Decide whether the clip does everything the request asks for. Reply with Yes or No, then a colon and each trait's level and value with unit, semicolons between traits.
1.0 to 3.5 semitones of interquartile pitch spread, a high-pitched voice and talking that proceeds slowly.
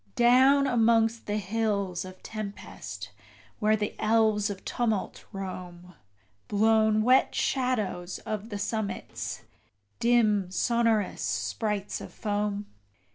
Yes: narrow, 2.5 semitones; high, 215 Hz; slow, 105 wpm